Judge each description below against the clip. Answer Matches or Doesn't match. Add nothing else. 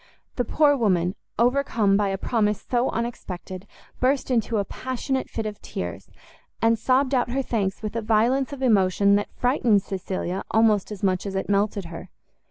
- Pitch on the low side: Doesn't match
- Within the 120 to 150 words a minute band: Doesn't match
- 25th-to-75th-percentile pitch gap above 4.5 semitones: Doesn't match